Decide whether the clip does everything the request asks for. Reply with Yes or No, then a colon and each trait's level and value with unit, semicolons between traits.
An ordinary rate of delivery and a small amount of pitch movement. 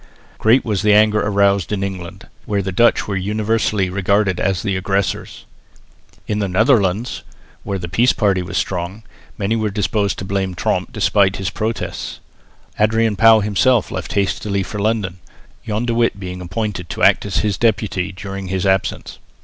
Yes: average, 165 wpm; narrow, 2.3 semitones